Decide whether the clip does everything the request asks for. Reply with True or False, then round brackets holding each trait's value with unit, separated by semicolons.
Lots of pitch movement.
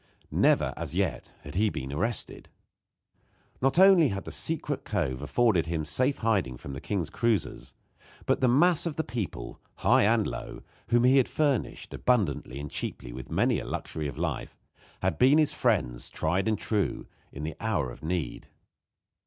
True (8.8 semitones)